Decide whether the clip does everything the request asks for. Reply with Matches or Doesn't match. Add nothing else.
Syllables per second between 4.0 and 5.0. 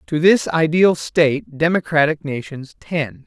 Matches